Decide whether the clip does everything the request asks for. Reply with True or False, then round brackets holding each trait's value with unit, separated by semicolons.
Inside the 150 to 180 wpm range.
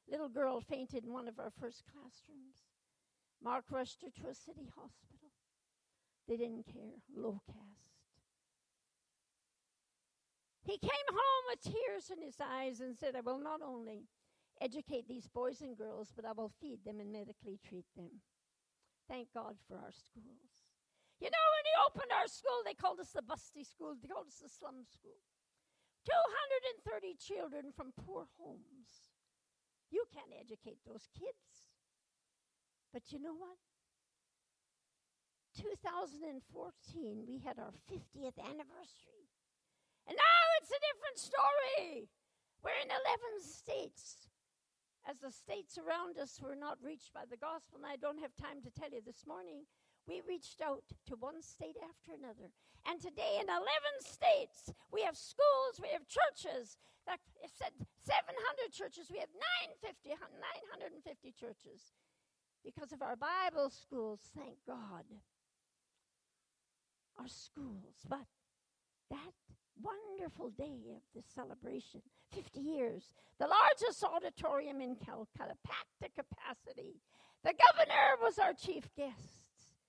False (140 wpm)